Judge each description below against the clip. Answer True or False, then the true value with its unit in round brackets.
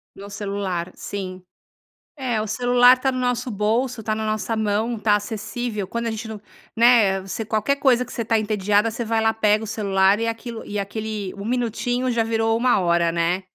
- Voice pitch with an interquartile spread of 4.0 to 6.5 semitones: False (2.6 semitones)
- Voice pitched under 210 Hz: False (220 Hz)